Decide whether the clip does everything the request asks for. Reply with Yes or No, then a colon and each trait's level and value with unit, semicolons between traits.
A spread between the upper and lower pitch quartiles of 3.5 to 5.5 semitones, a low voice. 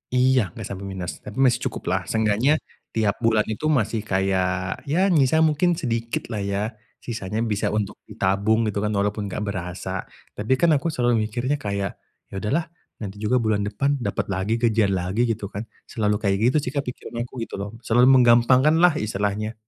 Yes: average, 3.9 semitones; low, 110 Hz